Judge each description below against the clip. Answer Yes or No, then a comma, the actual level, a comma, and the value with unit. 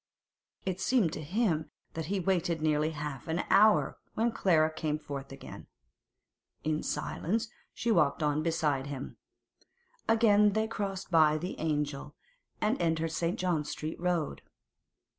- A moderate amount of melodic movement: Yes, average, 4.1 semitones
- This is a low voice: No, medium, 160 Hz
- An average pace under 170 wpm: Yes, average, 140 wpm